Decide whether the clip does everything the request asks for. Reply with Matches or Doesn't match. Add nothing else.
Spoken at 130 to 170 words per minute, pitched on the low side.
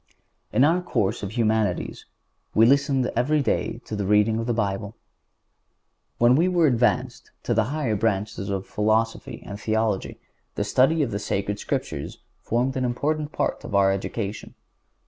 Matches